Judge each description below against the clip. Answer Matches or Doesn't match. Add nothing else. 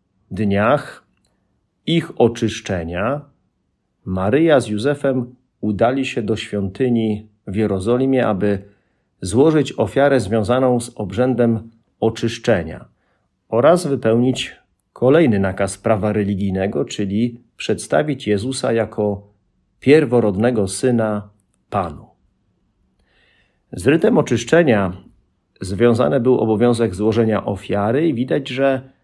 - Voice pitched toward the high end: Doesn't match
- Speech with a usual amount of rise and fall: Matches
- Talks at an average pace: Doesn't match